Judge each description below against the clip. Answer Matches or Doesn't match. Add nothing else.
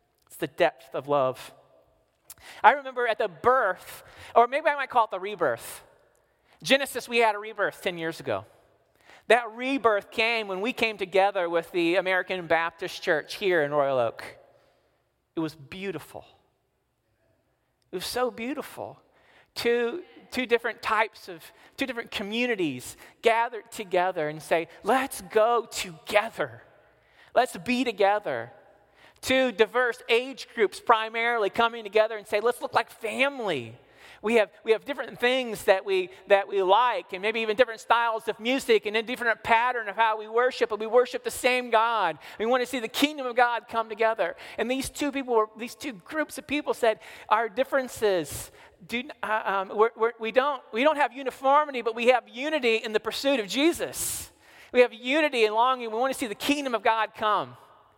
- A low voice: Doesn't match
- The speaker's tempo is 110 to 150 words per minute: Doesn't match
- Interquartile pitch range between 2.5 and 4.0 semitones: Matches